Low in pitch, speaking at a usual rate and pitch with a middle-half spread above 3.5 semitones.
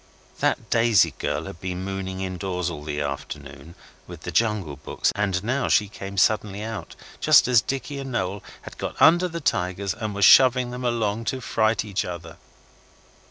Yes: low, 100 Hz; average, 175 wpm; average, 4.3 semitones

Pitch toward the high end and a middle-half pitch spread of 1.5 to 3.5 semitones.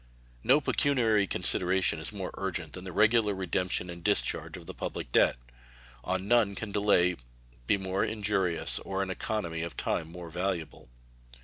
No: very low, 95 Hz; average, 2.9 semitones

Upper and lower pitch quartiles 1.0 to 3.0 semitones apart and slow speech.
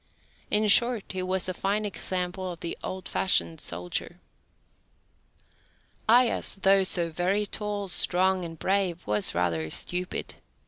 Yes: average, 2.7 semitones; slow, 130 wpm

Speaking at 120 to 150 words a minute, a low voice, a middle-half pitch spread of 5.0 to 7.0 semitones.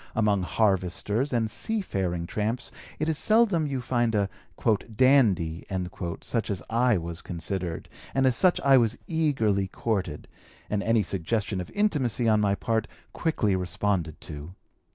Yes: average, 140 wpm; low, 110 Hz; wide, 5.4 semitones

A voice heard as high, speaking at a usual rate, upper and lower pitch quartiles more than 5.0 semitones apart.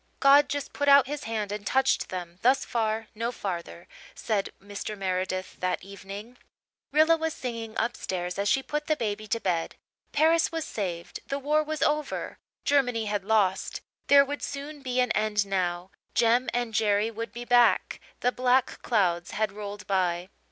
Yes: high, 225 Hz; average, 170 wpm; wide, 5.4 semitones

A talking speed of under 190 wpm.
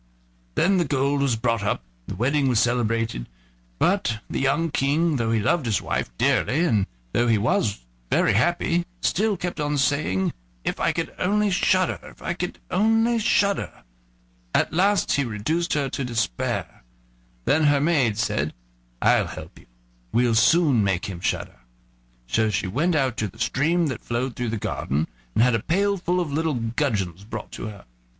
Yes: average, 175 wpm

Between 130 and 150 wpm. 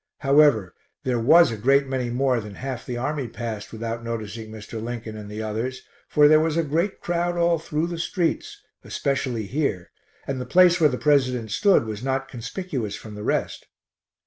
No: average, 185 wpm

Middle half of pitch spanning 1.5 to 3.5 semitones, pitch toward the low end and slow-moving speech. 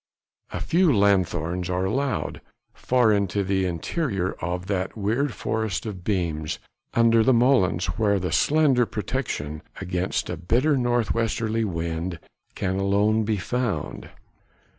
No: average, 4.5 semitones; low, 100 Hz; slow, 125 wpm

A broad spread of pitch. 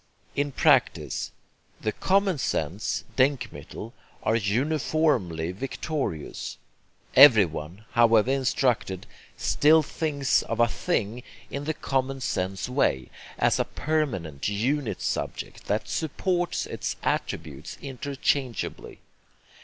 Yes: wide, 6.5 semitones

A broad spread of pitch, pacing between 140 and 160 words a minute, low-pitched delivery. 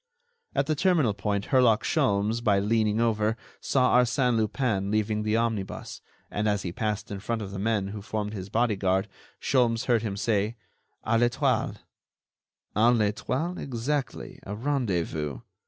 No: average, 2.9 semitones; average, 150 wpm; low, 110 Hz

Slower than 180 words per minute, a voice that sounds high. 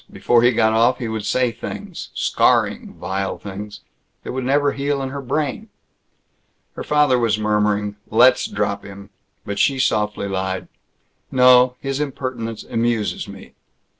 No: average, 145 wpm; low, 120 Hz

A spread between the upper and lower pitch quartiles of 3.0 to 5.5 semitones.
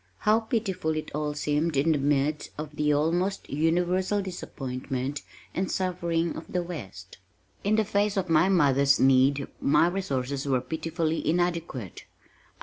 Yes: average, 4.2 semitones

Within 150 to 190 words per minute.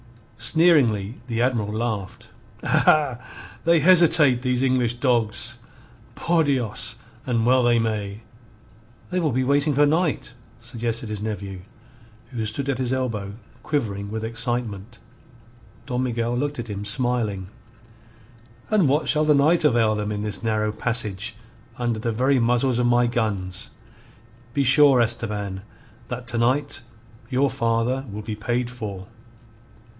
No: average, 140 wpm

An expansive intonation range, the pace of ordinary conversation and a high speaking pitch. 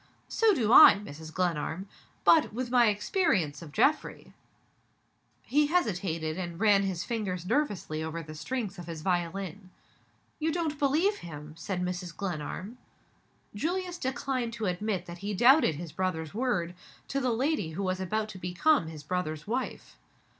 Yes: wide, 7.0 semitones; average, 155 wpm; high, 195 Hz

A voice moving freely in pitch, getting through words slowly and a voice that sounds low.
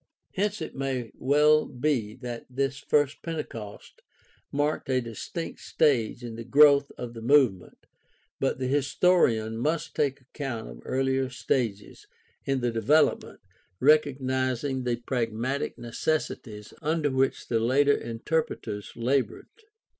No: average, 3.7 semitones; slow, 125 wpm; low, 130 Hz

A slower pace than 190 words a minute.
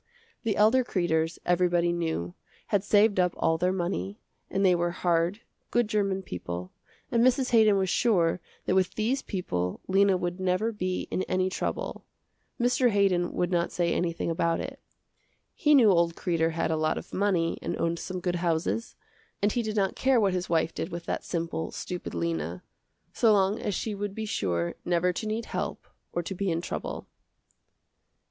Yes: average, 180 wpm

